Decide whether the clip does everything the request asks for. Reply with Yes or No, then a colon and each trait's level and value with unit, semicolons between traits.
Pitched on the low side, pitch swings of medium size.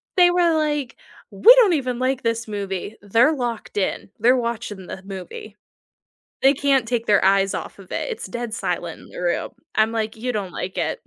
No: high, 230 Hz; average, 4.7 semitones